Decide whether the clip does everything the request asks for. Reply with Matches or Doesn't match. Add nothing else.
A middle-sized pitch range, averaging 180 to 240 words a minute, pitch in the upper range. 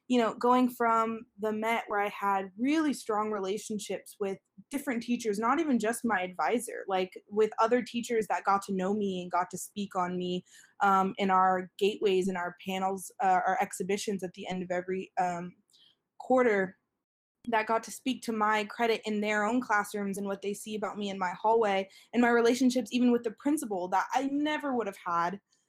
Matches